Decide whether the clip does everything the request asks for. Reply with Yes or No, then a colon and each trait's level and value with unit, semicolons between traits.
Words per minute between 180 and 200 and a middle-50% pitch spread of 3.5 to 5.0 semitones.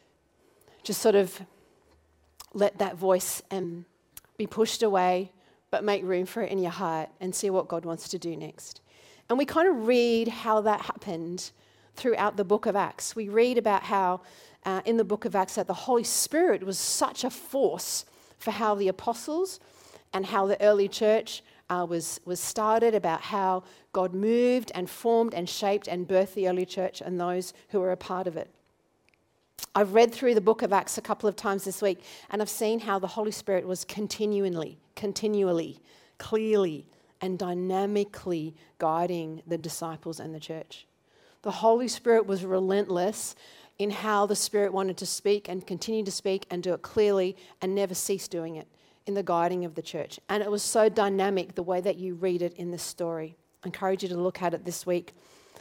No: average, 190 wpm; average, 2.8 semitones